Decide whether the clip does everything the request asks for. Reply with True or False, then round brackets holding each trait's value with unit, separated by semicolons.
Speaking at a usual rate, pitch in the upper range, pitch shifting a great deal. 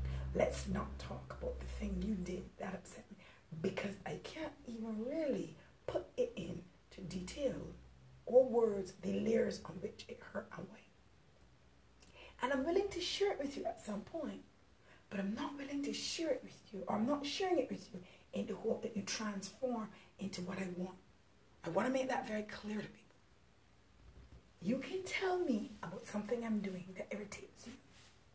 True (185 wpm; 210 Hz; 6.3 semitones)